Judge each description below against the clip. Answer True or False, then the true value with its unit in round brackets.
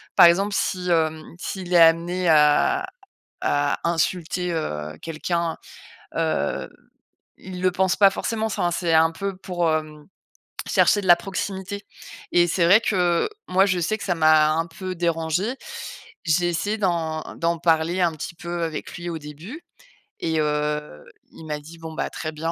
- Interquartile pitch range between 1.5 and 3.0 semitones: True (2.5 semitones)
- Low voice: False (170 Hz)